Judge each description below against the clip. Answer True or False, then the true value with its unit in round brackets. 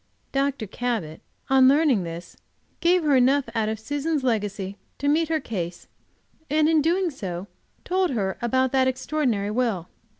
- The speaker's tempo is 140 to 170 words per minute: True (155 wpm)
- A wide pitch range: True (6.1 semitones)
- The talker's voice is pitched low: False (260 Hz)